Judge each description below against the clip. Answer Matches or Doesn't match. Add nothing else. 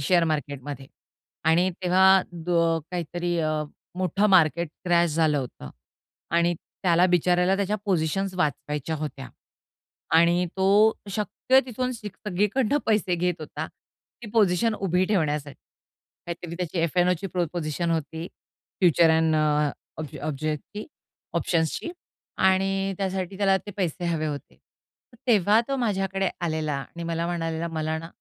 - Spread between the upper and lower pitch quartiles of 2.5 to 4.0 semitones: Matches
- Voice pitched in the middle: Matches